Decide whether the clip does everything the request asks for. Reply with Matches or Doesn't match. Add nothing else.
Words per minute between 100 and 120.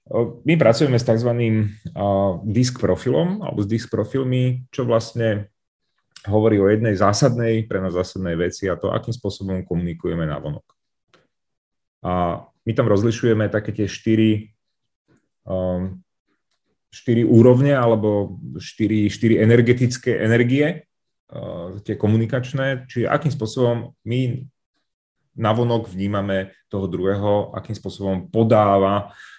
Matches